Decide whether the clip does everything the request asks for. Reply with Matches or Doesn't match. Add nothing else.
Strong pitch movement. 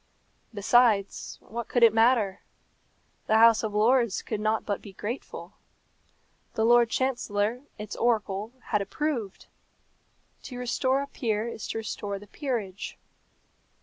Doesn't match